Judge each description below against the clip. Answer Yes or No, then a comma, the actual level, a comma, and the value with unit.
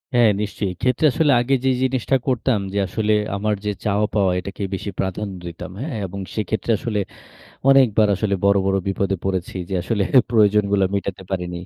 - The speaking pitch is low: Yes, low, 105 Hz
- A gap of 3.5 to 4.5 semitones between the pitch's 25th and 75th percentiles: No, average, 2.8 semitones